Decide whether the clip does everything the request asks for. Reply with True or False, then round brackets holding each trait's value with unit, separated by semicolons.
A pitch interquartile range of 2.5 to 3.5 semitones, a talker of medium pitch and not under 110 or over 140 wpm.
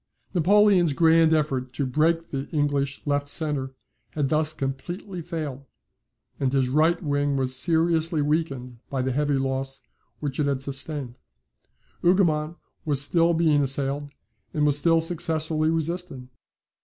True (3.2 semitones; 150 Hz; 135 wpm)